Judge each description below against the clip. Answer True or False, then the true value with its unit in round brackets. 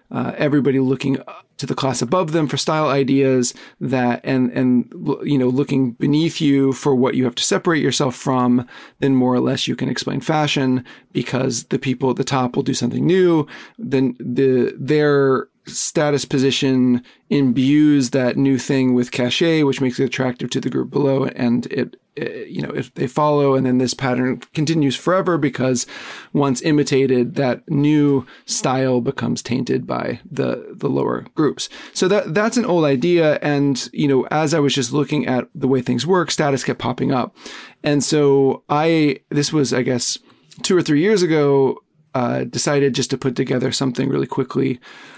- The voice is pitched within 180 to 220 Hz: False (135 Hz)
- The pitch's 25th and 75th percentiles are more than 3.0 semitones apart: False (2.5 semitones)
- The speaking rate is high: False (180 wpm)